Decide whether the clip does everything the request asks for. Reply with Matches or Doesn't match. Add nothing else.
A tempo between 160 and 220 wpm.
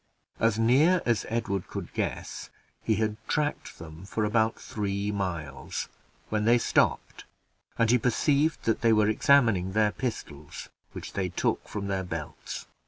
Doesn't match